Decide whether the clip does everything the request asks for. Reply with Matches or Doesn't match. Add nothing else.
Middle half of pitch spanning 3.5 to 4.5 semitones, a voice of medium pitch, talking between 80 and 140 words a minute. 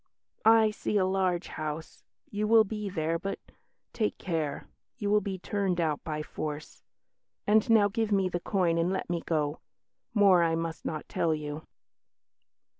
Doesn't match